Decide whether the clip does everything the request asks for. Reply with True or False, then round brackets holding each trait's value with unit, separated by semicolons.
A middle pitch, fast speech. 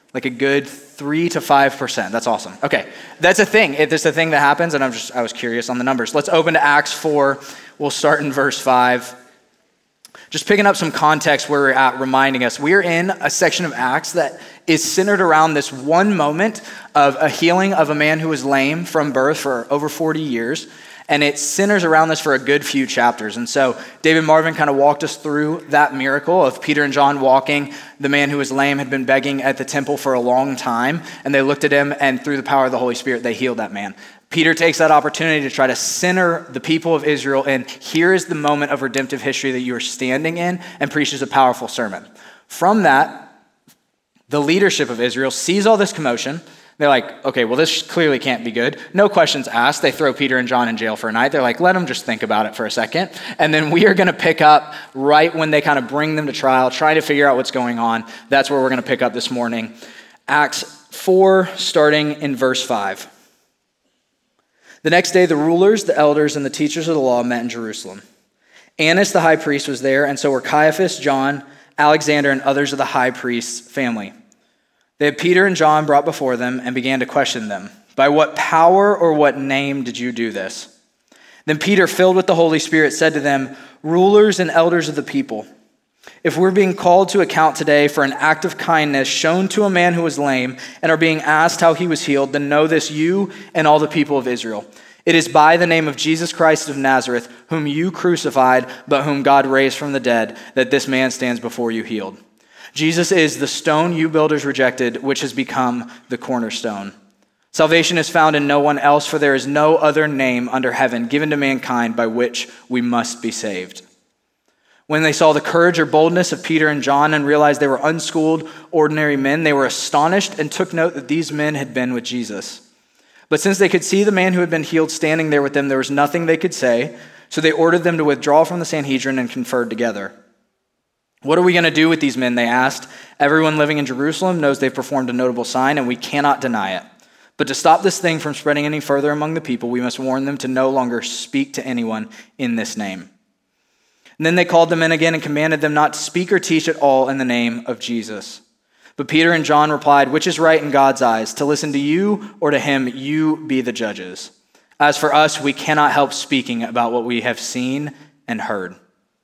True (145 Hz; 225 wpm)